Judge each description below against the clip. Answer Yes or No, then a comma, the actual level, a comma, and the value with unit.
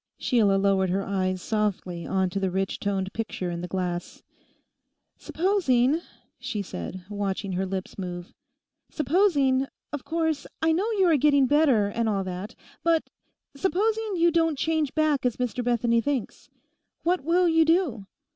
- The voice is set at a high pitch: Yes, high, 240 Hz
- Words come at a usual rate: Yes, average, 145 wpm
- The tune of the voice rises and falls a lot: Yes, wide, 8.7 semitones